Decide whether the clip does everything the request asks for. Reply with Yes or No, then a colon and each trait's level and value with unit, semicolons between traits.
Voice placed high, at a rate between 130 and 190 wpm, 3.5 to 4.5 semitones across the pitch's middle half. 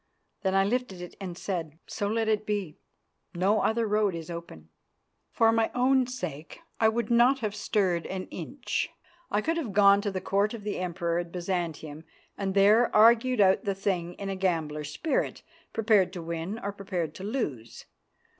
Yes: high, 195 Hz; average, 180 wpm; average, 4.1 semitones